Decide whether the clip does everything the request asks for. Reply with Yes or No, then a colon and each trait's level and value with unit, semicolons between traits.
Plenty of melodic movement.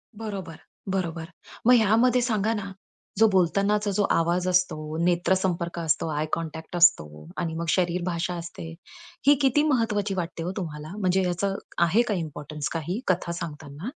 No: average, 3.5 semitones